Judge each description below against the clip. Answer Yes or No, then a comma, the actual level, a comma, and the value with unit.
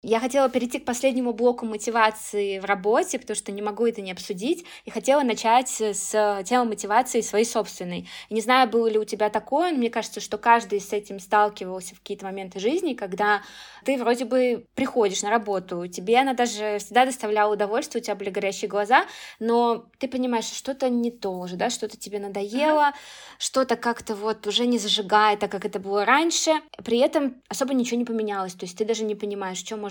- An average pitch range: Yes, average, 3.3 semitones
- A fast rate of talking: Yes, fast, 195 wpm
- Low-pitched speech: No, high, 220 Hz